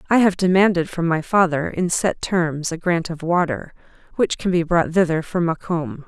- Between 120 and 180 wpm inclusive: No, average, 200 wpm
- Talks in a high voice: No, medium, 170 Hz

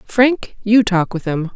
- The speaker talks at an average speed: Yes, average, 195 wpm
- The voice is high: Yes, high, 205 Hz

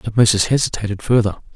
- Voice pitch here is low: Yes, low, 110 Hz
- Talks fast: No, slow, 115 wpm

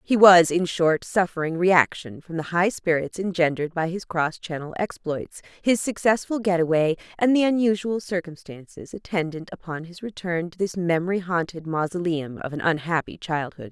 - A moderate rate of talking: Yes, average, 160 wpm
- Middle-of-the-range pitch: Yes, medium, 175 Hz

